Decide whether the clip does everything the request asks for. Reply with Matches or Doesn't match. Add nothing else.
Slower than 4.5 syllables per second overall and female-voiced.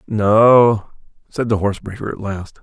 Doesn't match